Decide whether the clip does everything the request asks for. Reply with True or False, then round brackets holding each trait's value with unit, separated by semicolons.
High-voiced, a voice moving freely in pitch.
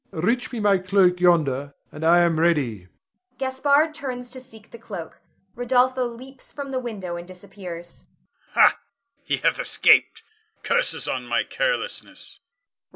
True (215 Hz; 7.0 semitones)